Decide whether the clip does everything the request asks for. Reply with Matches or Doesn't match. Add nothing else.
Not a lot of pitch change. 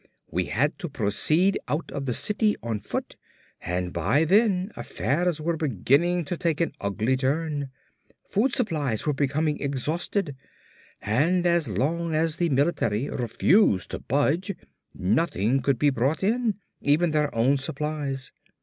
Doesn't match